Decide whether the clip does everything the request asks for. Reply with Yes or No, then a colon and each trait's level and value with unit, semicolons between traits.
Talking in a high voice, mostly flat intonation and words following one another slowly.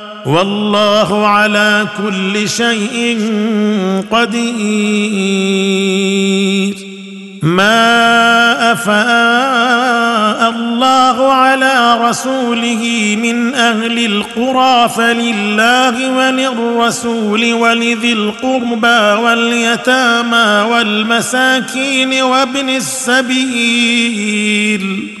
Yes: high, 235 Hz; narrow, 2.2 semitones; slow, 50 wpm